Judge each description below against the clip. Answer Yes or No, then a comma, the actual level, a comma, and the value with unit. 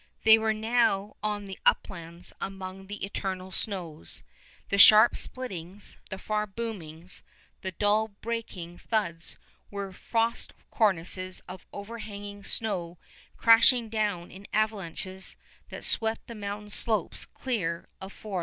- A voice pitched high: Yes, high, 200 Hz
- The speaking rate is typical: No, slow, 125 wpm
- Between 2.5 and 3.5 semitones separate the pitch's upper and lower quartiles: Yes, average, 2.8 semitones